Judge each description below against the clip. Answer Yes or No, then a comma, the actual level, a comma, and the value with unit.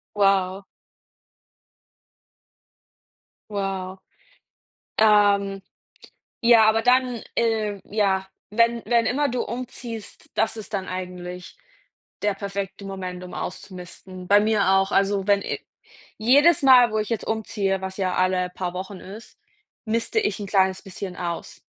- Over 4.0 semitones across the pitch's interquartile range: No, average, 2.9 semitones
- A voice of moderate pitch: No, high, 200 Hz